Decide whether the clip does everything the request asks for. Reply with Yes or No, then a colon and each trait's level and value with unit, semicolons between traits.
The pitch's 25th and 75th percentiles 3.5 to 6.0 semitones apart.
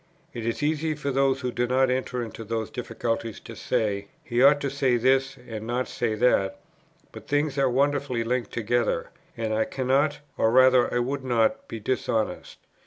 No: average, 2.9 semitones